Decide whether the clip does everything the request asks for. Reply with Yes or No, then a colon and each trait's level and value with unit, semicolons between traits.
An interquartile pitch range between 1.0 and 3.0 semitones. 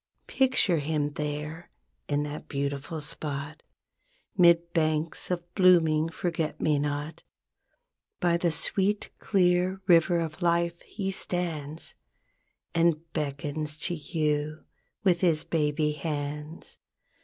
Yes: narrow, 2.5 semitones